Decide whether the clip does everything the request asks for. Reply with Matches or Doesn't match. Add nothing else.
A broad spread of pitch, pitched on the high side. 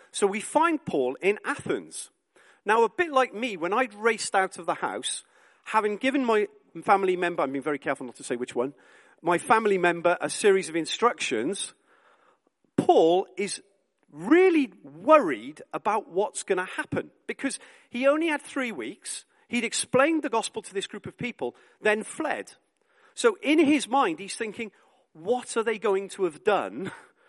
Matches